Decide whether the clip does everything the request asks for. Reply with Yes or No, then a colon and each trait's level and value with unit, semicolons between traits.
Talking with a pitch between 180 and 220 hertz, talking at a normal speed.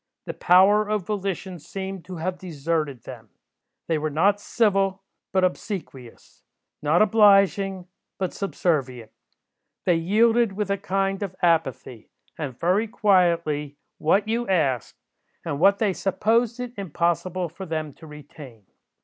No: medium, 185 Hz; slow, 130 wpm